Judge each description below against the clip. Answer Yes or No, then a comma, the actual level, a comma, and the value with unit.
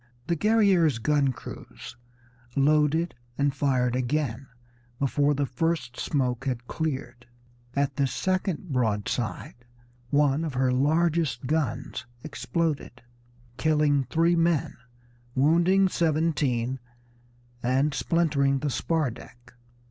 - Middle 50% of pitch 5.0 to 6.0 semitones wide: No, average, 4.0 semitones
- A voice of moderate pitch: Yes, medium, 145 Hz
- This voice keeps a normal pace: No, slow, 105 wpm